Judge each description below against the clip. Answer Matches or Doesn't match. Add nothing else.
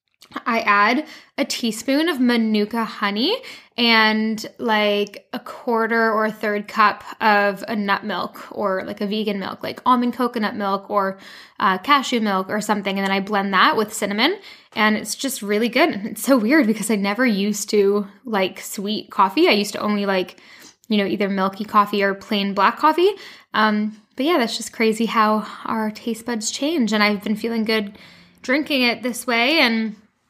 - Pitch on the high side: Matches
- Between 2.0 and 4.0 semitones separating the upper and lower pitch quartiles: Matches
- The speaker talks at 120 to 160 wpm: Doesn't match